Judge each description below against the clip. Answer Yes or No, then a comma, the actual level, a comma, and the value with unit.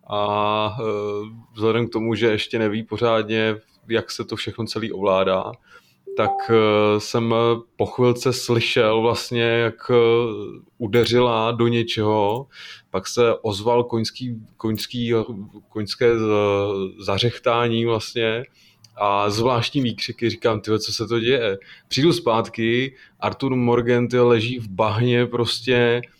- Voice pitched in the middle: No, low, 115 Hz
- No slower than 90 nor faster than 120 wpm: Yes, slow, 115 wpm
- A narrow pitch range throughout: Yes, narrow, 1.8 semitones